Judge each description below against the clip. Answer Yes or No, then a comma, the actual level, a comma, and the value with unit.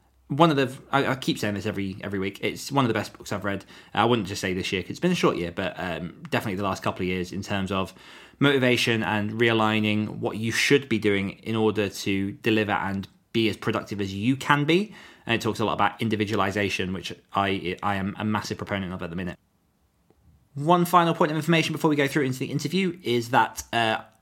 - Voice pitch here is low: Yes, low, 105 Hz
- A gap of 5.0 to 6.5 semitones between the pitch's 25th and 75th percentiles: Yes, average, 5.3 semitones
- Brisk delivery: Yes, fast, 235 wpm